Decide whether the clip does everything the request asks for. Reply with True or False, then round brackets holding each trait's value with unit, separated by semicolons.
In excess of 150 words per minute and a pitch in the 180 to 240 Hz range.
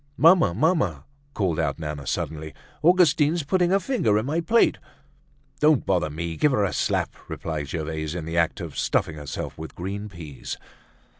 False (165 wpm; 95 Hz)